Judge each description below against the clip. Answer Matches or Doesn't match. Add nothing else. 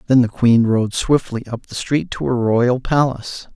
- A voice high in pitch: Doesn't match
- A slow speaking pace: Doesn't match